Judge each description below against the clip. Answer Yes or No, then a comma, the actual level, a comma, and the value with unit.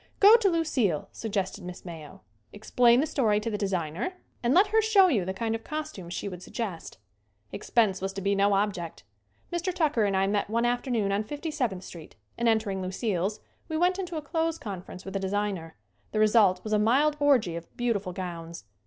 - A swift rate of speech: Yes, fast, 210 wpm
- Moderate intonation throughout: No, wide, 6.6 semitones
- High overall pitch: Yes, high, 210 Hz